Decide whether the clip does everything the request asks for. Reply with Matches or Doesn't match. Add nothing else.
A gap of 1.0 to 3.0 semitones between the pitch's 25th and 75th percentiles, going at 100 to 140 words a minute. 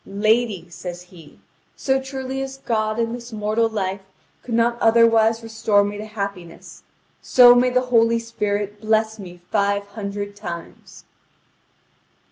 Matches